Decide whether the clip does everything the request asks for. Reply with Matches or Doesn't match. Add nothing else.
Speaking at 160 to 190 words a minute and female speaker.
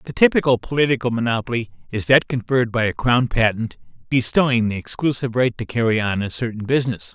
Doesn't match